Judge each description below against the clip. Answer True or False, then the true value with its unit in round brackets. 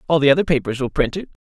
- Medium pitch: True (150 Hz)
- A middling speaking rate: False (285 wpm)